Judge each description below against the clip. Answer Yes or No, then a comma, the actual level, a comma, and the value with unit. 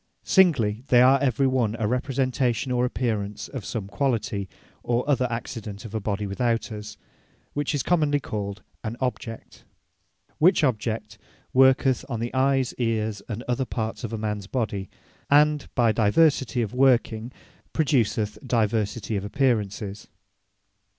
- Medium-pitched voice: No, low, 120 Hz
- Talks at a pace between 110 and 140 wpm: Yes, slow, 135 wpm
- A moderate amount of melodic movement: Yes, average, 3.6 semitones